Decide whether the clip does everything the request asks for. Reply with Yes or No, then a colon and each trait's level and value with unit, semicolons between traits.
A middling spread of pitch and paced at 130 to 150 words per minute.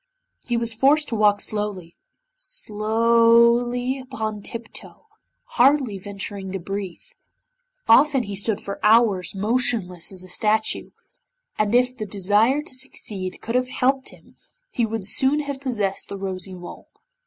Yes: average, 4.1 semitones; average, 140 wpm